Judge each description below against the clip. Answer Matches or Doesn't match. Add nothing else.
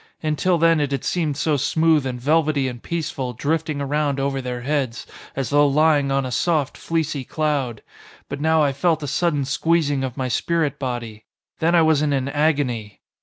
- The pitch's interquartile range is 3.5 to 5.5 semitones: Doesn't match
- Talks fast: Doesn't match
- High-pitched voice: Doesn't match